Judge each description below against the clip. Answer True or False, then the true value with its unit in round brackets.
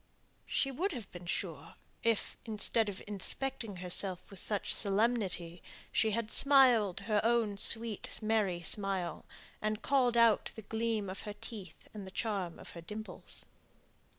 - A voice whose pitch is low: False (210 Hz)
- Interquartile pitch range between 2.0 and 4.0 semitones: True (3.3 semitones)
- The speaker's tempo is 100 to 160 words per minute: True (150 wpm)